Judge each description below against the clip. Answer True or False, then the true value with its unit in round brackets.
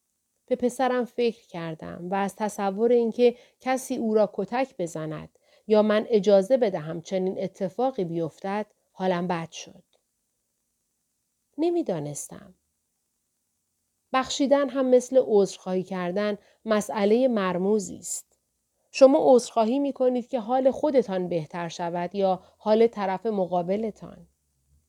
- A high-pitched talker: True (210 Hz)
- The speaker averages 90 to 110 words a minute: True (105 wpm)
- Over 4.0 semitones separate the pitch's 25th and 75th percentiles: True (5.2 semitones)